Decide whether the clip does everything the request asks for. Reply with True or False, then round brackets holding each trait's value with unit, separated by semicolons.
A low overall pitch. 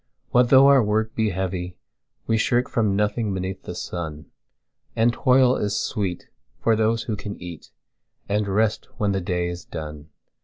True (105 Hz)